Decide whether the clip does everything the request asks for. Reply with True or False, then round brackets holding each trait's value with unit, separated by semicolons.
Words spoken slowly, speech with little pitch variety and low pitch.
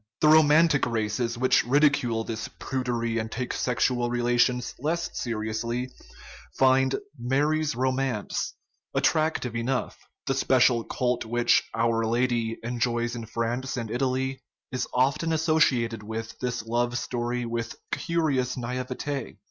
True (130 wpm; 2.3 semitones; 125 Hz)